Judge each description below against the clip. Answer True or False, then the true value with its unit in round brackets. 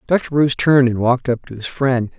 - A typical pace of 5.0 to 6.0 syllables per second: False (6.3 syllables/s)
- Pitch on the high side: False (130 Hz)